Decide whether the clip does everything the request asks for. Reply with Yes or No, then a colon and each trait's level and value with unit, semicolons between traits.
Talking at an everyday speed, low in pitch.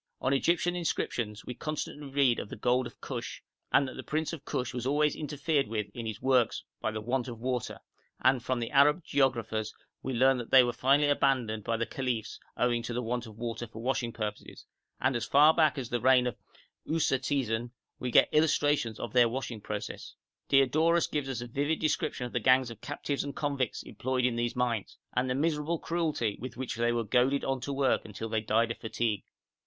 No: fast, 210 wpm; low, 125 Hz